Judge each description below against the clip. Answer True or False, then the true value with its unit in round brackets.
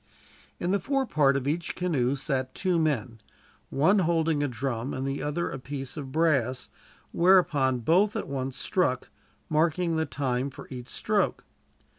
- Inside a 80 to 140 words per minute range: False (160 wpm)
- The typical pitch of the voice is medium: True (145 Hz)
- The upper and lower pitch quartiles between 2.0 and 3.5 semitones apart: False (4.3 semitones)